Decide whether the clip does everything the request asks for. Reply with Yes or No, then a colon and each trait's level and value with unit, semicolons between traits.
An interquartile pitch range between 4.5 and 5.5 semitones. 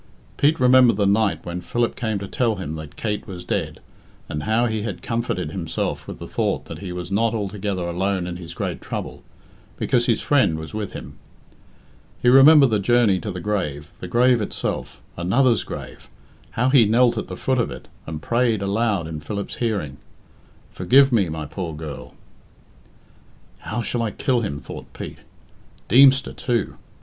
Yes: average, 5.2 semitones